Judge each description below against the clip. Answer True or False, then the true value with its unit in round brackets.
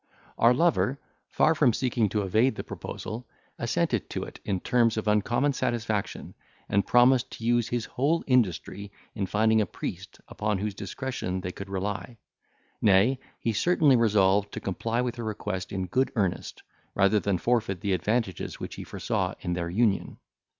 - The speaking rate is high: False (165 wpm)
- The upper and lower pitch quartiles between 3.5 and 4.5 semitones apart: True (3.8 semitones)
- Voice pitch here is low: True (110 Hz)